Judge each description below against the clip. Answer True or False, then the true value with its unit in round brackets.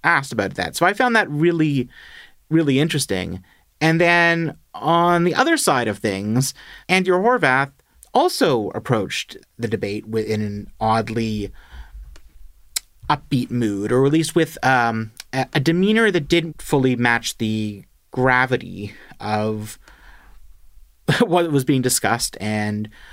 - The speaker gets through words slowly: True (125 wpm)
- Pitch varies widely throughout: True (7.3 semitones)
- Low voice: True (125 Hz)